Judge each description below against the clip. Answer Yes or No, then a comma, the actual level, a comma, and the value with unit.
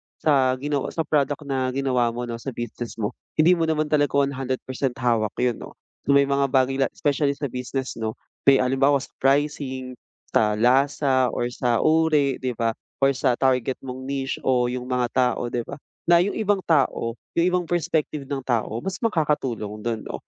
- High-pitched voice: No, low, 135 Hz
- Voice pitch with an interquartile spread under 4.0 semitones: Yes, average, 2.8 semitones